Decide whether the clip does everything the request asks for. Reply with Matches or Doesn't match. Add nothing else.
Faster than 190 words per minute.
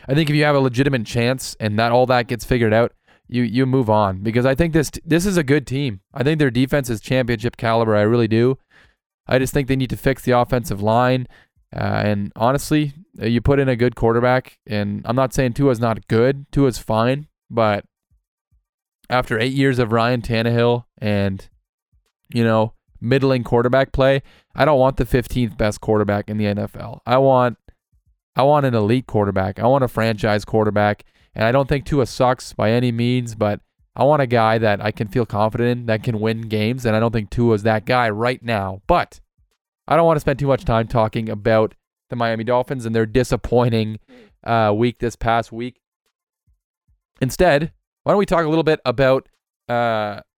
Matches